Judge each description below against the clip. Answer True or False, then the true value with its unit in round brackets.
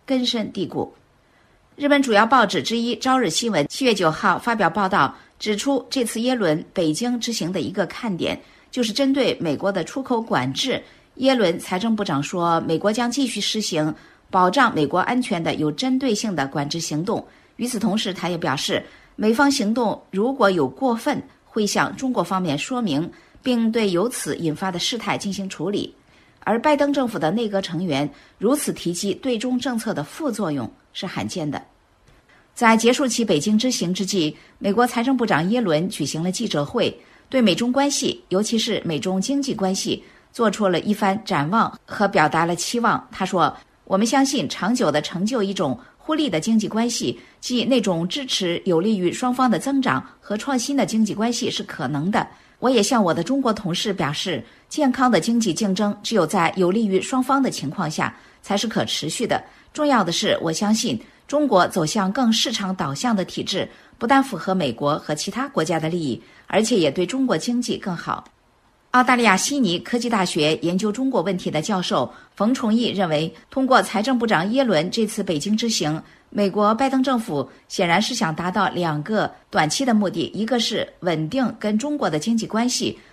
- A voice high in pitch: True (210 Hz)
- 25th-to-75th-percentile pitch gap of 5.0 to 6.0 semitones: True (5.3 semitones)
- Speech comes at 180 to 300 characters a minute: True (280 characters per minute)